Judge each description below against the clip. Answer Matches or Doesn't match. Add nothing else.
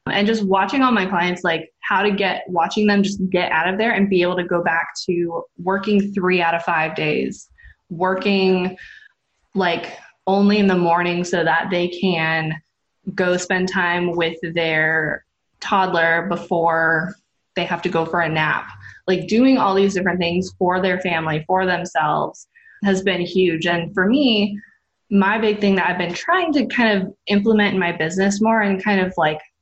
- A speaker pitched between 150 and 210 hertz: Matches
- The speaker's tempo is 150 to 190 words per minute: Matches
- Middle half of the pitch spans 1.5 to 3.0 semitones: Matches